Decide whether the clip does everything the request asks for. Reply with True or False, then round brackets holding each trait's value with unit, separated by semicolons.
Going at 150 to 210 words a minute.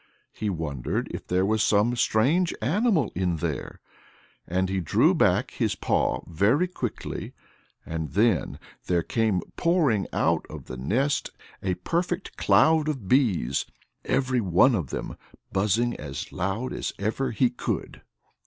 False (140 wpm)